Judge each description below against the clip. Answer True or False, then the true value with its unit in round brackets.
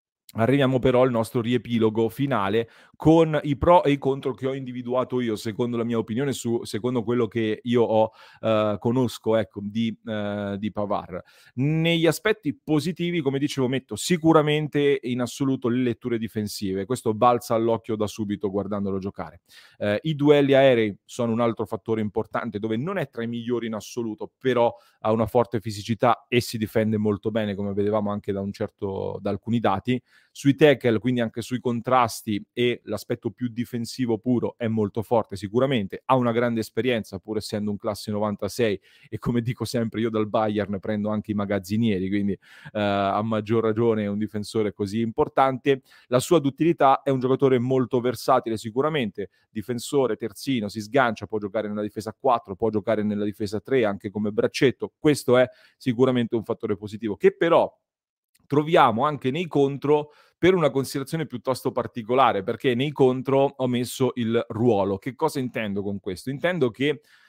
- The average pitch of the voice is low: True (115 Hz)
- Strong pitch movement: False (3.5 semitones)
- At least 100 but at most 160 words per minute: False (170 wpm)